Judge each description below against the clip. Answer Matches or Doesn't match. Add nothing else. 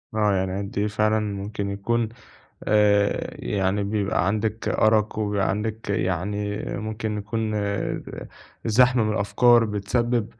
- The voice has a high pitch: Doesn't match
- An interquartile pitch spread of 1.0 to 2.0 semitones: Matches